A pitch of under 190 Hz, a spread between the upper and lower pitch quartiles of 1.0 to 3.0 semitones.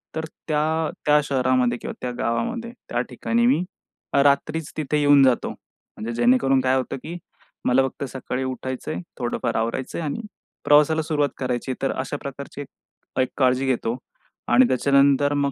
Yes: medium, 140 Hz; average, 2.7 semitones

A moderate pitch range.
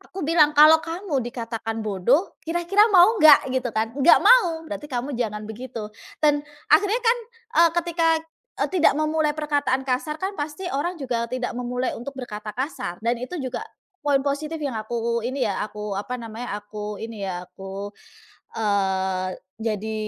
No: wide, 6.1 semitones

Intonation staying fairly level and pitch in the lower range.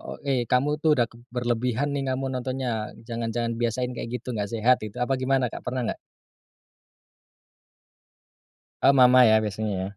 Yes: narrow, 2.0 semitones; low, 125 Hz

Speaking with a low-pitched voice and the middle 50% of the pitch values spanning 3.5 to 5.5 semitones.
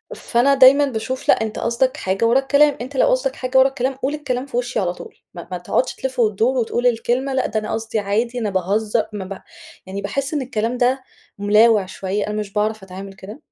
No: high, 235 Hz; average, 4.0 semitones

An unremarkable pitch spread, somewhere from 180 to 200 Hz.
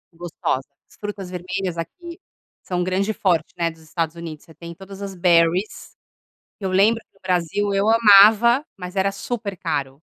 Yes: average, 3.1 semitones; medium, 185 Hz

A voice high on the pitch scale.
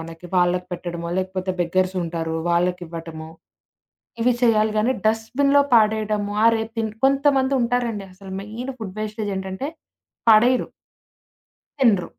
Yes: high, 210 Hz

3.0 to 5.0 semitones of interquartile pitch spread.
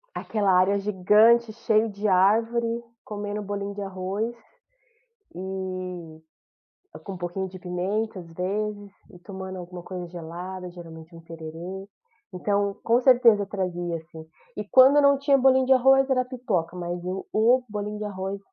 Yes: average, 3.4 semitones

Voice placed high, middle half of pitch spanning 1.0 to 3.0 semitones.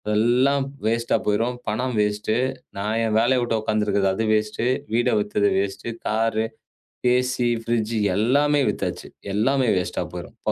No: low, 115 Hz; narrow, 2.5 semitones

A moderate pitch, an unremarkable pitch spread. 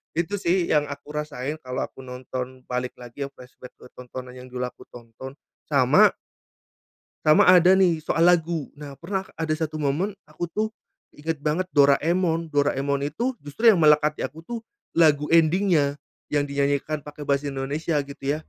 Yes: medium, 150 Hz; average, 3.2 semitones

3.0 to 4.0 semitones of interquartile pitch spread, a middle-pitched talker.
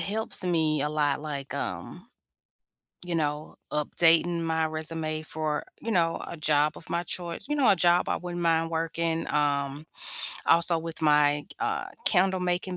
No: narrow, 2.4 semitones; medium, 165 Hz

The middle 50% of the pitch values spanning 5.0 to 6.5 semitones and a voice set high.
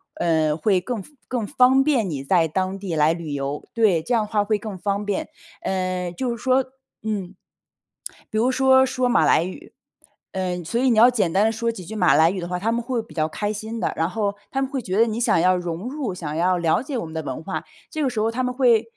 Yes: wide, 5.4 semitones; high, 205 Hz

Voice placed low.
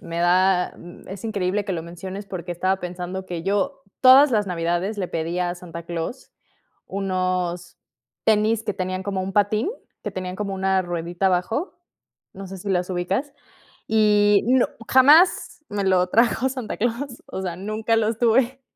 No: high, 190 Hz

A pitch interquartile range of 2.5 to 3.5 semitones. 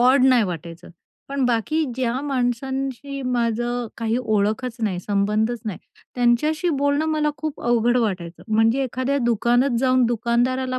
Yes: average, 2.8 semitones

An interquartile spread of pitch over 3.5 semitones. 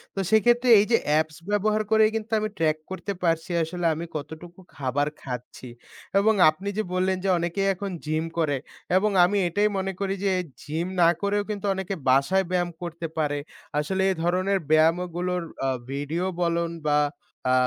Yes: average, 4.0 semitones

